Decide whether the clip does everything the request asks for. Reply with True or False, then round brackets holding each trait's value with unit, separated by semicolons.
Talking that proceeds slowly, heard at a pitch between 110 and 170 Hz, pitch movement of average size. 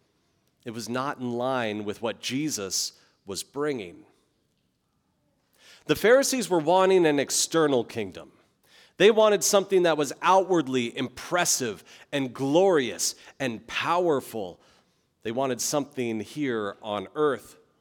False (115 wpm; 135 Hz; 5.7 semitones)